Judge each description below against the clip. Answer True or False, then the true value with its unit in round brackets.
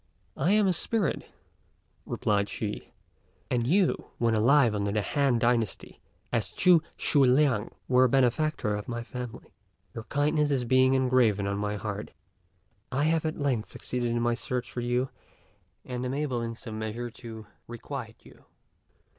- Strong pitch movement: False (3.7 semitones)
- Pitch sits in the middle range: False (125 Hz)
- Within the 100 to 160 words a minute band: True (155 wpm)